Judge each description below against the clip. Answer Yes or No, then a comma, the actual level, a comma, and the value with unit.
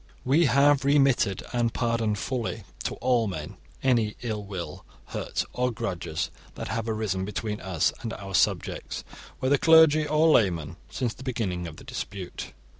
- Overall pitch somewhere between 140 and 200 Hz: No, low, 115 Hz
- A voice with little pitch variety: No, average, 5.2 semitones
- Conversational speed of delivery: Yes, average, 155 wpm